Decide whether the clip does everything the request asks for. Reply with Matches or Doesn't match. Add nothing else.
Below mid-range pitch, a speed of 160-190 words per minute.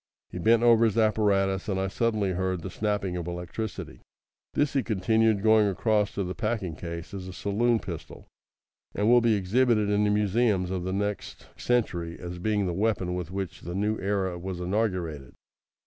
Matches